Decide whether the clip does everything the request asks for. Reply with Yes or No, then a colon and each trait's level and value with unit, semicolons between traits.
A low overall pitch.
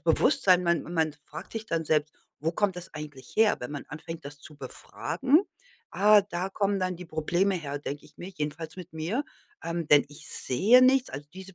No: medium, 170 Hz